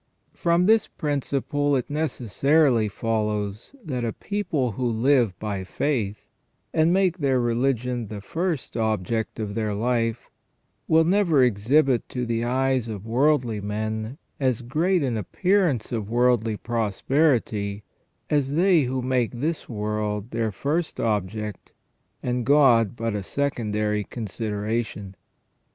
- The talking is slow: Yes, slow, 125 wpm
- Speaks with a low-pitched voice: Yes, low, 120 Hz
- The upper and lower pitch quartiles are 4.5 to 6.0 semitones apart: Yes, average, 4.9 semitones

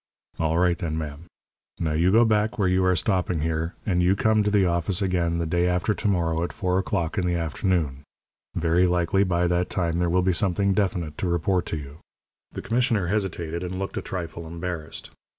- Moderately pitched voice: No, very low, 90 Hz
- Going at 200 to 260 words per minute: Yes, fast, 205 wpm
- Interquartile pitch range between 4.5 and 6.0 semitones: No, narrow, 2.4 semitones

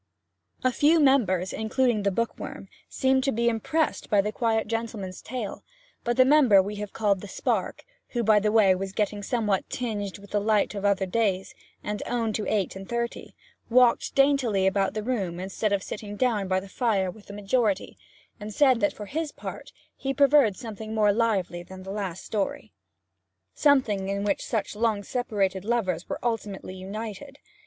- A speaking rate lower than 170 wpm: No, average, 180 wpm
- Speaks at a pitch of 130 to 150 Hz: No, high, 210 Hz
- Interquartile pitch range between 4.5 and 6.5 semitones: No, average, 3.3 semitones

